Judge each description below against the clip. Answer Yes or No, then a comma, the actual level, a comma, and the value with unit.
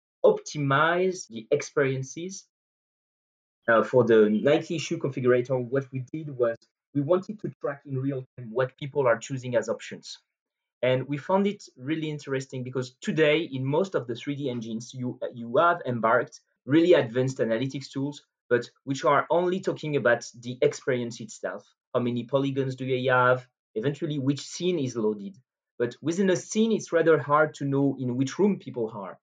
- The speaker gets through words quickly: No, average, 170 wpm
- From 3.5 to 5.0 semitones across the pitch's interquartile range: Yes, average, 4.1 semitones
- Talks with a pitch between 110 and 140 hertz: Yes, low, 135 Hz